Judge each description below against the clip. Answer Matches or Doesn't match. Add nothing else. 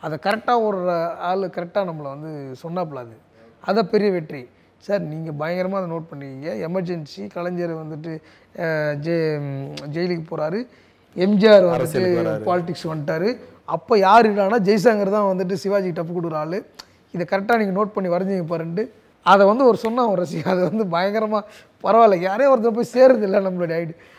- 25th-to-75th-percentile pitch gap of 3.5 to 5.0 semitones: Matches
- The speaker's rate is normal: Doesn't match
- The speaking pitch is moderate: Matches